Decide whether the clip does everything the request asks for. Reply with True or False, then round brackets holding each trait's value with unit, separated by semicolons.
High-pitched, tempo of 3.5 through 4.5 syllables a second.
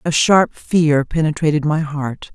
False (155 Hz; 4.0 syllables/s)